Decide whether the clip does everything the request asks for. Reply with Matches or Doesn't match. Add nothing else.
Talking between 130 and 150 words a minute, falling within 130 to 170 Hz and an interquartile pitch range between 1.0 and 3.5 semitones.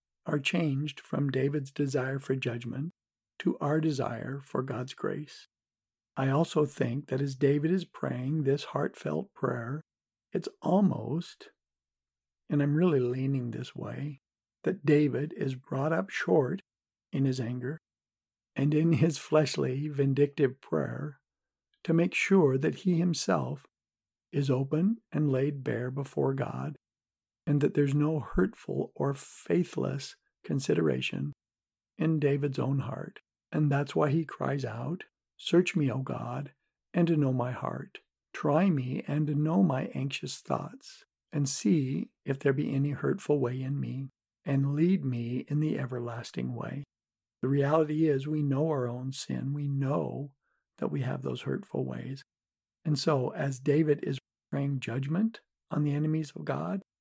Matches